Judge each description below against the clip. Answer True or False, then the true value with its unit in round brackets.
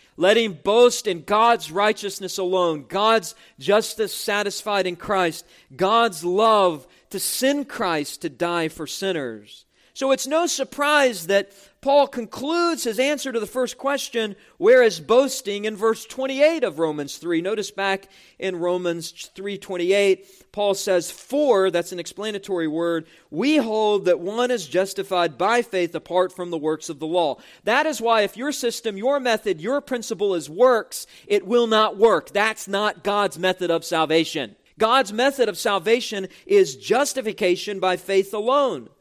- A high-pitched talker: True (205 Hz)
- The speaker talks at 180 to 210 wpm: False (155 wpm)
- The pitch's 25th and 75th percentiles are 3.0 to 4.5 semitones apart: False (5.0 semitones)